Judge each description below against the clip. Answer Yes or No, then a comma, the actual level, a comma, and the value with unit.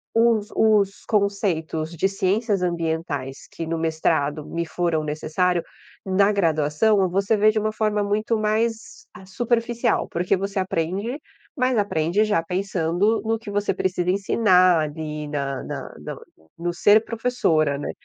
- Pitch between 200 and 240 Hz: No, high, 190 Hz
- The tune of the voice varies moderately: Yes, average, 4.8 semitones